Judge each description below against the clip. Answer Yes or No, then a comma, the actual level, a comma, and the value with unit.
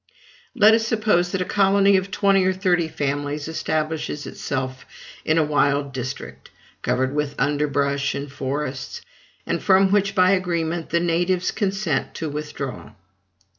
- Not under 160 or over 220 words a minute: No, average, 140 wpm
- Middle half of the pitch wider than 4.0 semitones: Yes, average, 4.8 semitones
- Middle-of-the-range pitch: Yes, medium, 160 Hz